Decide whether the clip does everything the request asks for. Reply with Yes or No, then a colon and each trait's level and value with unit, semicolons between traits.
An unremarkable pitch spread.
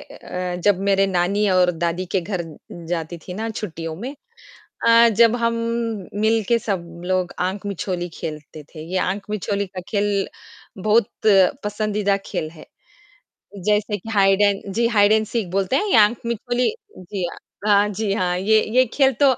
Yes: average, 3.0 semitones